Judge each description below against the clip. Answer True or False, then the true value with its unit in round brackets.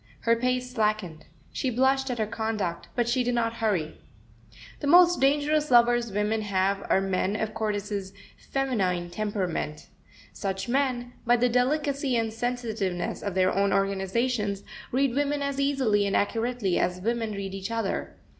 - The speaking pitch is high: True (225 Hz)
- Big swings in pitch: False (4.1 semitones)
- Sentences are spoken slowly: False (155 wpm)